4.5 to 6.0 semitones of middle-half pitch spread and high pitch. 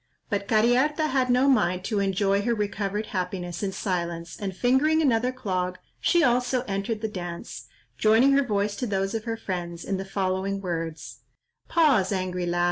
Yes: average, 4.8 semitones; high, 200 Hz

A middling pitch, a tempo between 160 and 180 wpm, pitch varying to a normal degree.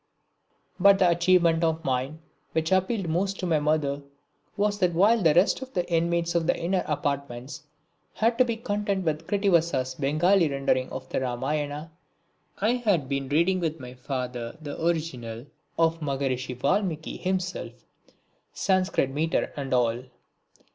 No: medium, 160 Hz; average, 145 wpm; average, 5.0 semitones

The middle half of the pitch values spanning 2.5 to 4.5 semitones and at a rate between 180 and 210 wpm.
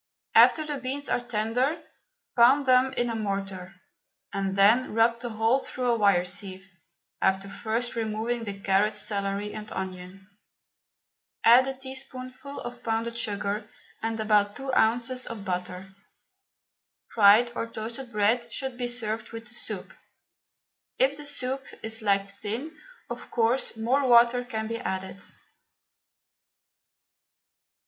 No: average, 3.4 semitones; slow, 135 wpm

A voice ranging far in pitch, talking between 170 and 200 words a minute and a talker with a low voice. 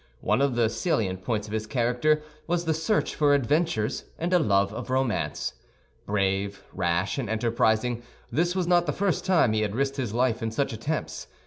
Yes: wide, 6.1 semitones; average, 190 wpm; low, 120 Hz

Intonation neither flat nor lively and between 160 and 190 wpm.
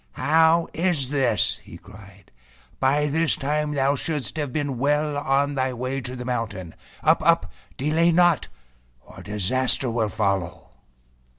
No: average, 3.3 semitones; average, 150 wpm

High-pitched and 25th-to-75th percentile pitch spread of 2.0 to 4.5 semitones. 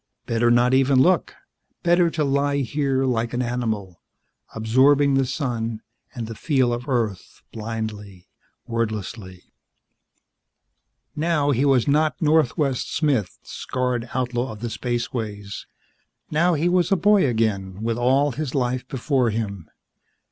No: low, 125 Hz; average, 4.0 semitones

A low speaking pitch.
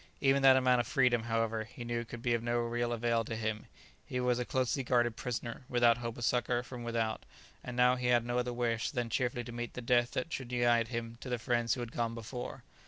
Yes: low, 120 Hz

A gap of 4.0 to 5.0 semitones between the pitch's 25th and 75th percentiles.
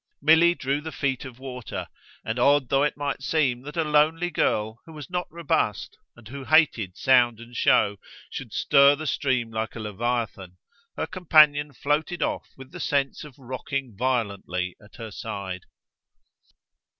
Yes: average, 4.7 semitones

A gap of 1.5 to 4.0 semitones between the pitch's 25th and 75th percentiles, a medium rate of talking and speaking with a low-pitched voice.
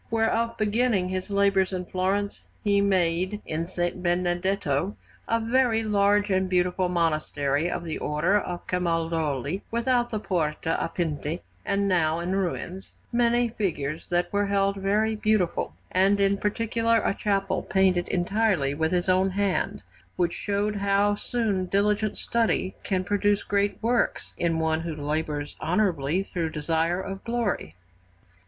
No: average, 3.2 semitones; average, 145 wpm; high, 190 Hz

